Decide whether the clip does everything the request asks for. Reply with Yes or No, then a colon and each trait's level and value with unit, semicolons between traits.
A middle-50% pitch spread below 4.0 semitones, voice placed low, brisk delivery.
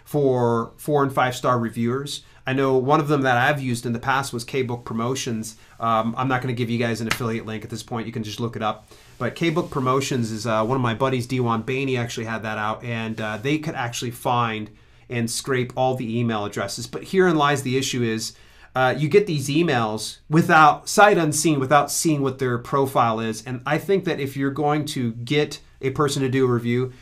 Yes: average, 3.5 semitones; low, 125 Hz; fast, 225 wpm